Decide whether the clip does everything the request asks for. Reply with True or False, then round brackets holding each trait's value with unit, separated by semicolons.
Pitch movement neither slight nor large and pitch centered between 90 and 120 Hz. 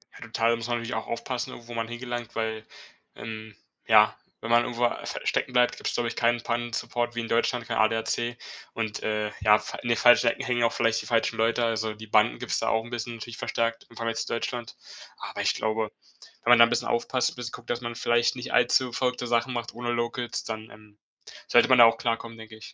False (1.1 semitones; 115 Hz)